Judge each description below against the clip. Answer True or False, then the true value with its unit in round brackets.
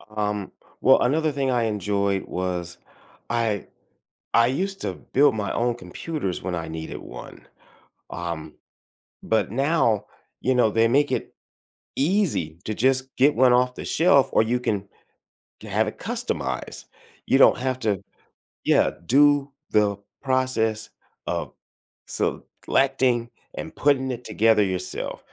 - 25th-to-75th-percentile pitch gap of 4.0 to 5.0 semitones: True (4.7 semitones)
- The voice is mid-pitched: False (115 Hz)